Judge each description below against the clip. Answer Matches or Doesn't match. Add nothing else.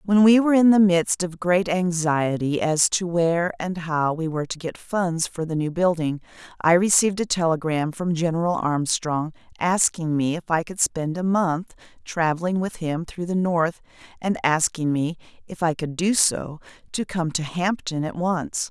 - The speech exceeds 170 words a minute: Matches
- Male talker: Doesn't match